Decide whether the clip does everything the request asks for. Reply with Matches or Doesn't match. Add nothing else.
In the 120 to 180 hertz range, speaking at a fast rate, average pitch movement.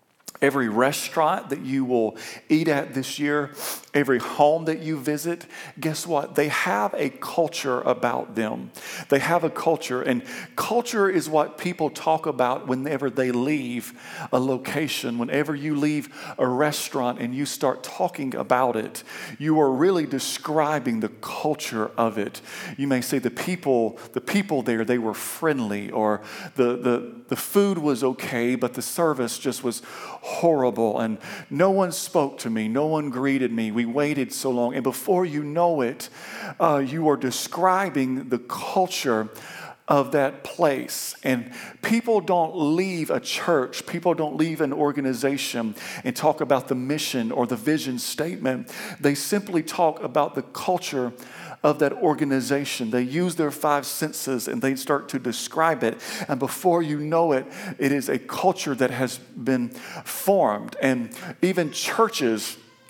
Doesn't match